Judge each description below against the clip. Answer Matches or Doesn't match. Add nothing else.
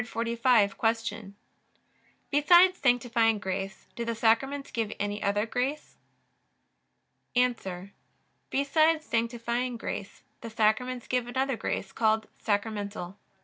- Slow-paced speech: Matches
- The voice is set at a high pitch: Matches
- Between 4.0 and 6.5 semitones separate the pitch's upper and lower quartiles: Doesn't match